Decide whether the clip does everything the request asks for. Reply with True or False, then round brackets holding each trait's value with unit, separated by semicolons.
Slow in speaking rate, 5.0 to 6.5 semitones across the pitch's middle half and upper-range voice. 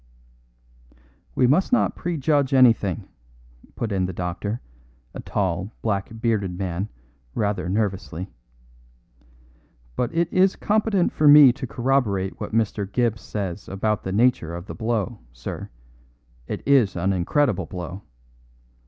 False (125 wpm; 5.5 semitones; 105 Hz)